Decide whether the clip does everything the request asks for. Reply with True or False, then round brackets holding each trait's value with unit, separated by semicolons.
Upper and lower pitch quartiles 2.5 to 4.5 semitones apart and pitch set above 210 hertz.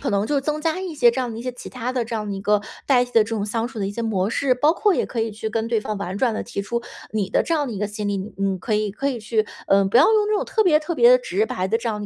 False (5.1 semitones; 230 Hz)